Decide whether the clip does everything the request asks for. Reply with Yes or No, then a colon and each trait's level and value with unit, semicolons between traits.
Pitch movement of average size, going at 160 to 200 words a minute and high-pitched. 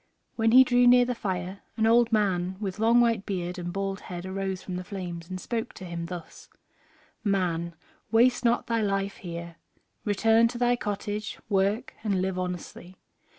Yes: average, 3.9 semitones; average, 175 wpm; high, 195 Hz